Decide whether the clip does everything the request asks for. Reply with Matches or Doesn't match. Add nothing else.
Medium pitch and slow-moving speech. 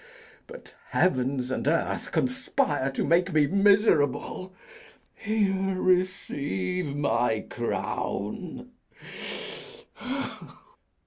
Matches